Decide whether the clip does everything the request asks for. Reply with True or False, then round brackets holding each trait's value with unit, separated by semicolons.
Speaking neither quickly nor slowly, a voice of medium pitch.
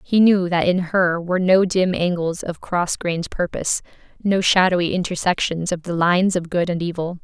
True (190 wpm; 180 Hz)